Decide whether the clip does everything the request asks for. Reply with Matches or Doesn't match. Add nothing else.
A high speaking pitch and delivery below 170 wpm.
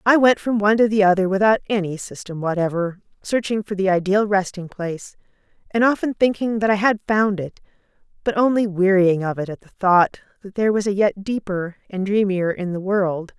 Doesn't match